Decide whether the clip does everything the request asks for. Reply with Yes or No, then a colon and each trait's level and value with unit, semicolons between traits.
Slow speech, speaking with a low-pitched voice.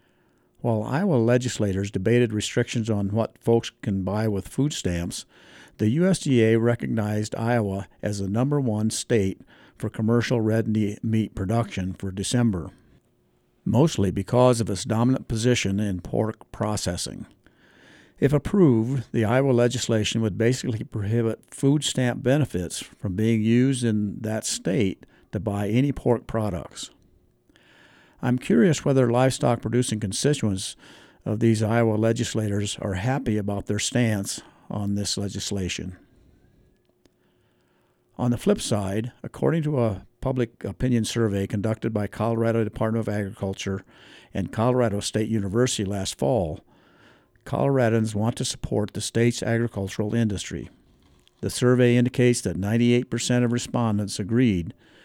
Yes: slow, 125 wpm; low, 115 Hz